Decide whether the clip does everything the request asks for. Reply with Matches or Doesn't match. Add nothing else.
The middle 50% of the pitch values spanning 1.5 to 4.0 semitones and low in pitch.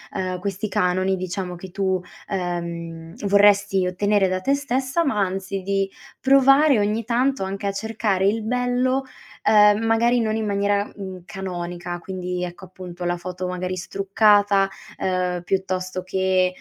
Doesn't match